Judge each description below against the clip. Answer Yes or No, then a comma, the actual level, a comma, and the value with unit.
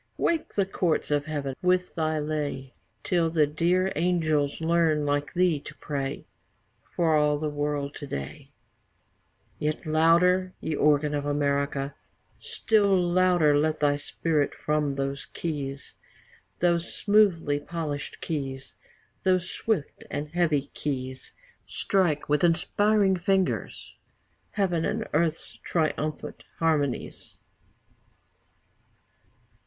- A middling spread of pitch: Yes, average, 3.3 semitones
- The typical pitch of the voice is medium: Yes, medium, 155 Hz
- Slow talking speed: Yes, slow, 110 wpm